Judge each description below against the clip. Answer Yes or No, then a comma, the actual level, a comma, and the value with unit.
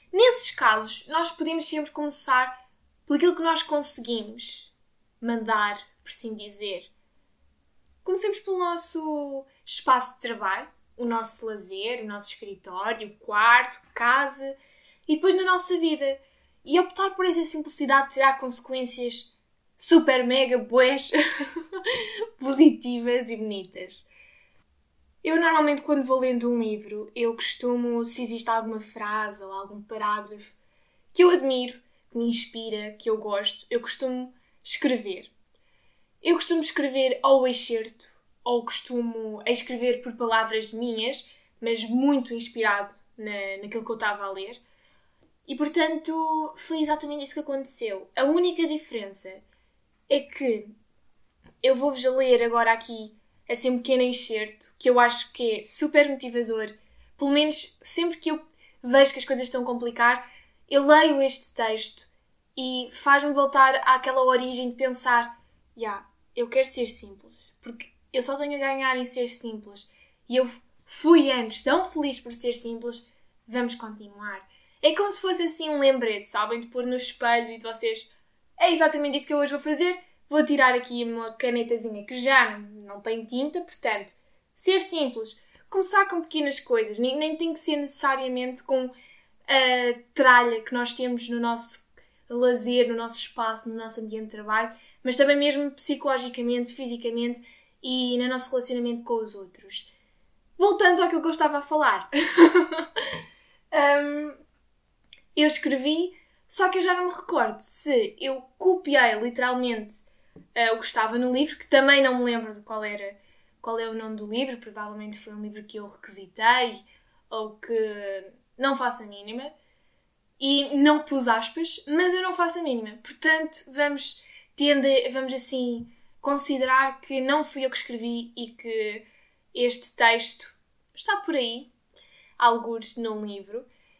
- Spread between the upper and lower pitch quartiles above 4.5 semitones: No, average, 4.2 semitones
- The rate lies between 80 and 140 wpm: No, average, 150 wpm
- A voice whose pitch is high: Yes, very high, 250 Hz